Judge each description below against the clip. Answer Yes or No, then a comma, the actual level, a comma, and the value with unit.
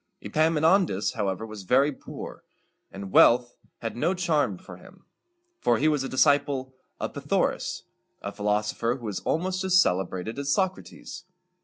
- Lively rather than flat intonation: Yes, wide, 6.8 semitones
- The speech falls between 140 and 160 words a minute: Yes, average, 155 wpm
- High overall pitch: No, low, 130 Hz